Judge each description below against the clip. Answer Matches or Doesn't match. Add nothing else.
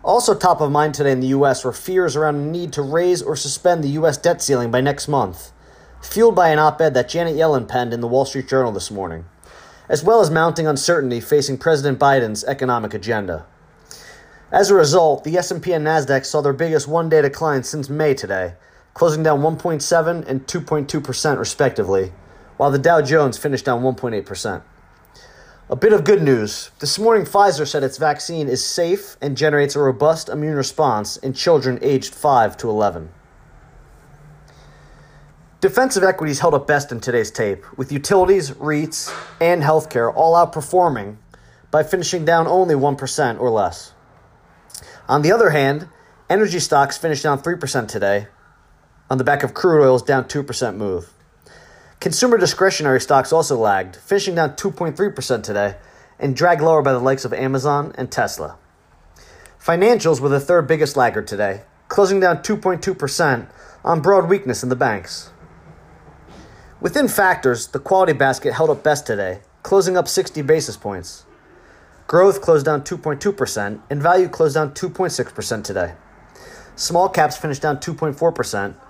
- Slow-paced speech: Doesn't match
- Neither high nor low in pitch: Matches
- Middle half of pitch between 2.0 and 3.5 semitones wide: Doesn't match